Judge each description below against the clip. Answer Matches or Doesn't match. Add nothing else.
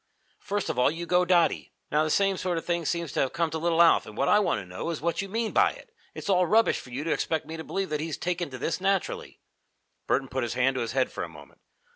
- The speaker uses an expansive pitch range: Doesn't match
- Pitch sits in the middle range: Matches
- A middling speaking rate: Doesn't match